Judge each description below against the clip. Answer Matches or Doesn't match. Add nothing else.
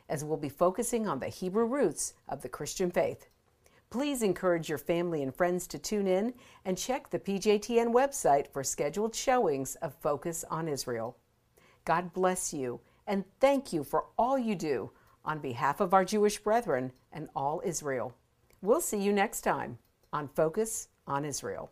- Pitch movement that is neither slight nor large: Doesn't match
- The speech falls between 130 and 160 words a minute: Doesn't match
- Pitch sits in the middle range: Matches